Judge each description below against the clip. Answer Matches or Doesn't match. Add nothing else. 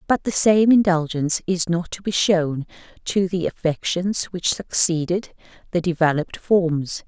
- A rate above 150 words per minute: Doesn't match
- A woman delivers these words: Matches